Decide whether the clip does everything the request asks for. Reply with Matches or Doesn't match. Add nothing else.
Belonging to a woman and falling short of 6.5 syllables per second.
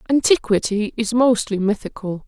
Matches